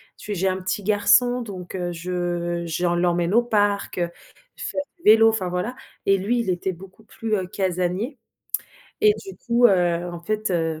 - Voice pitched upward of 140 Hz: Yes, high, 190 Hz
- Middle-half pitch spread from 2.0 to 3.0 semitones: No, average, 3.7 semitones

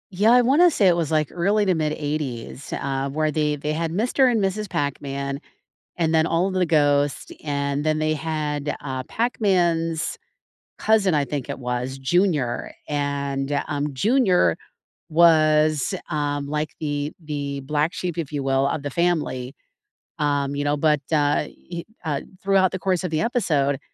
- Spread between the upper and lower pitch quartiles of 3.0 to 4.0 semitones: Yes, average, 3.4 semitones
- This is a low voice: No, medium, 150 Hz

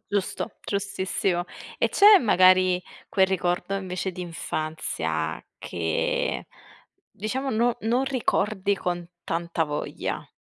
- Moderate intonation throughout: Yes, average, 3.2 semitones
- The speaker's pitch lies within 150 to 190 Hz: Yes, medium, 185 Hz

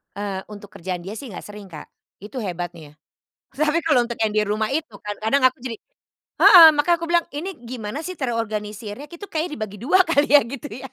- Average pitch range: No, wide, 6.0 semitones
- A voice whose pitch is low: No, high, 230 Hz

